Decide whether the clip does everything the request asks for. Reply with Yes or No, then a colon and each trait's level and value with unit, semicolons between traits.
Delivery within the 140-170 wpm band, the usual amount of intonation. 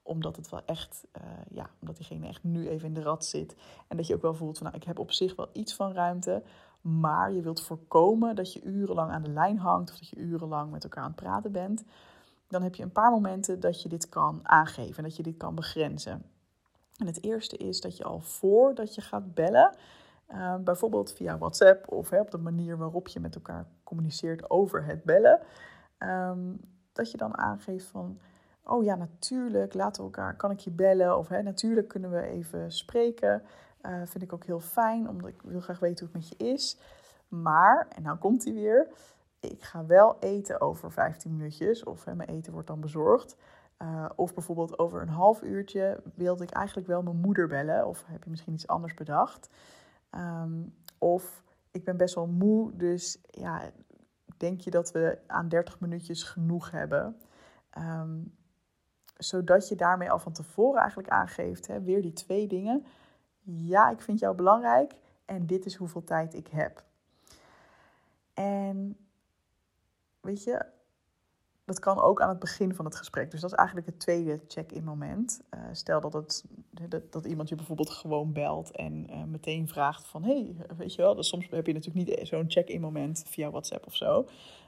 No: average, 195 wpm; average, 3.4 semitones